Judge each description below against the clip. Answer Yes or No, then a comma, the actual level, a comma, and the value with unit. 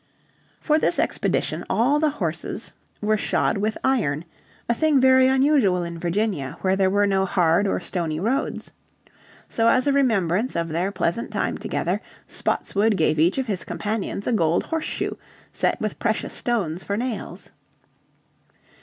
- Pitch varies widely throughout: Yes, wide, 6.3 semitones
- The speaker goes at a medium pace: Yes, average, 155 wpm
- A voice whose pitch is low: No, high, 205 Hz